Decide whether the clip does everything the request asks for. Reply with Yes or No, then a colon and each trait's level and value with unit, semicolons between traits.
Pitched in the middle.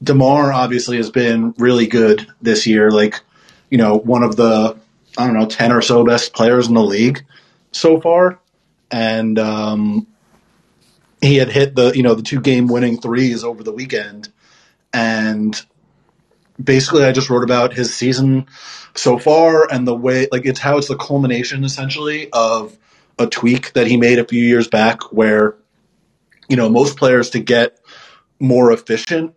No: low, 125 Hz